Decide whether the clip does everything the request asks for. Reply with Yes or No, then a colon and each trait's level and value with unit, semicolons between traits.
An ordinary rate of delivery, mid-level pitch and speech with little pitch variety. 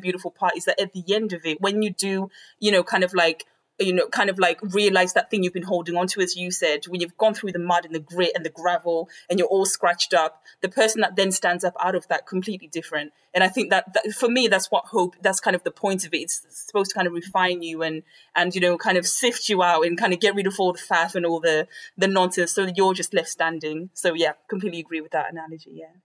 No: fast, 280 wpm; medium, 180 Hz; narrow, 2.3 semitones